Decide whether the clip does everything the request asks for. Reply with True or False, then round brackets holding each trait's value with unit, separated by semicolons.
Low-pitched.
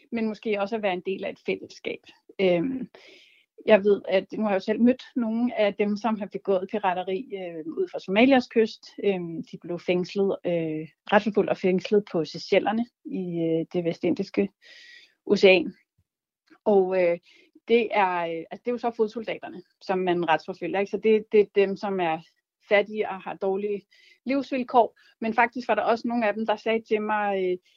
False (205 Hz)